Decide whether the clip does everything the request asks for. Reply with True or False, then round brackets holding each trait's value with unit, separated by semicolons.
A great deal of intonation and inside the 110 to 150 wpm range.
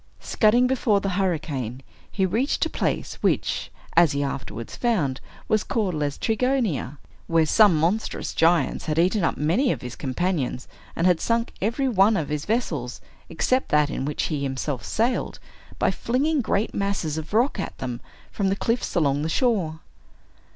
False (7.0 semitones; 165 wpm)